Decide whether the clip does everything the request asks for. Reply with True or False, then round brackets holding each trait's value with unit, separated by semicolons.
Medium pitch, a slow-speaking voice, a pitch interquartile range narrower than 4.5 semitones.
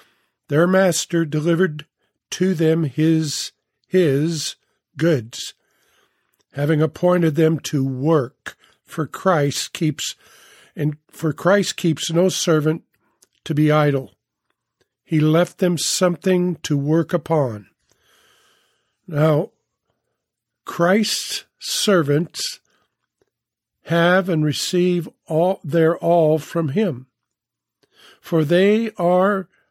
True (165 Hz; 95 wpm; 2.8 semitones)